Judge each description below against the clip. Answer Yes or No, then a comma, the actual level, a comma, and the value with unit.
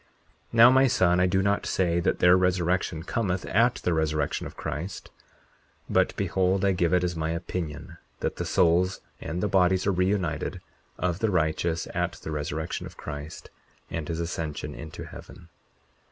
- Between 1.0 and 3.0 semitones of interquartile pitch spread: Yes, narrow, 2.6 semitones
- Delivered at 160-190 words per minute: Yes, average, 170 wpm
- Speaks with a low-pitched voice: Yes, very low, 90 Hz